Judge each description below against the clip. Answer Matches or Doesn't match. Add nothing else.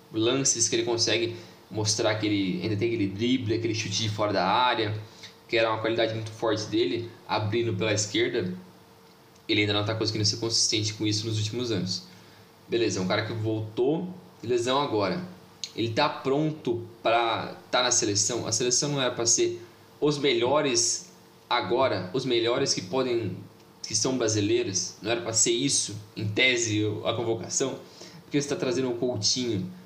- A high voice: Doesn't match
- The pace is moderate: Matches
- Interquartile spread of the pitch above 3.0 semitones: Doesn't match